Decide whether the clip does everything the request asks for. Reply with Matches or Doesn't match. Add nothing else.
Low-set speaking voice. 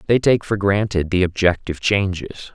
Matches